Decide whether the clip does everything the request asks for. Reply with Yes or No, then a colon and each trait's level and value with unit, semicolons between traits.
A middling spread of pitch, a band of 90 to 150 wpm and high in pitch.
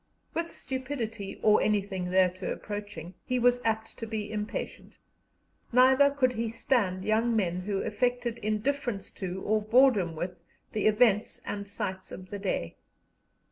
Yes: average, 4.1 semitones; average, 140 wpm; high, 215 Hz